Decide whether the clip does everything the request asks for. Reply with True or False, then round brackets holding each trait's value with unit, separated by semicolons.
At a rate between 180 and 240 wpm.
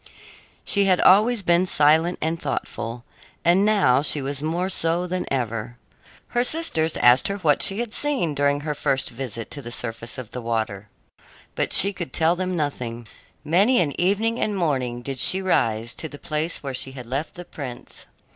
True (185 wpm)